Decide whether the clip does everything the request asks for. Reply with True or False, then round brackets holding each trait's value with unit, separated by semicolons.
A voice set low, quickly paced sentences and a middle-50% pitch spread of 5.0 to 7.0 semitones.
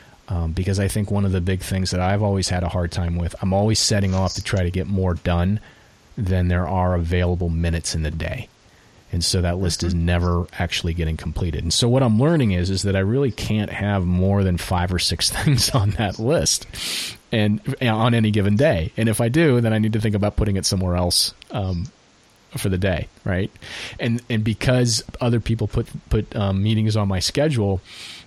False (95 Hz; 215 wpm; 3.7 semitones)